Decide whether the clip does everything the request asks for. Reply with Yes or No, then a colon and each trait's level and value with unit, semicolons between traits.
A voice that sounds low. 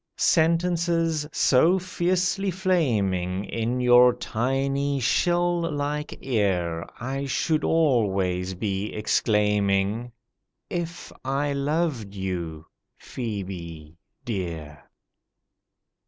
Yes: low, 125 Hz